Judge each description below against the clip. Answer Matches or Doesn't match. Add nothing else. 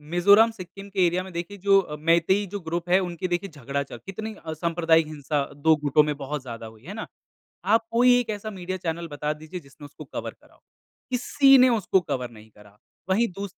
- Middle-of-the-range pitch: Matches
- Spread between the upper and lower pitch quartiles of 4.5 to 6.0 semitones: Matches